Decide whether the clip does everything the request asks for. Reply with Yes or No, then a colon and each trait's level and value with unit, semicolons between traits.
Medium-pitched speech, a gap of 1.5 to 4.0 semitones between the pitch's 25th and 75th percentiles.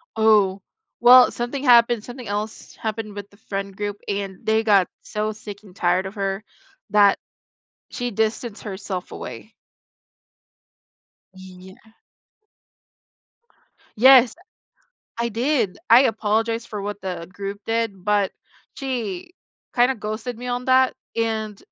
No: high, 215 Hz; average, 2.8 semitones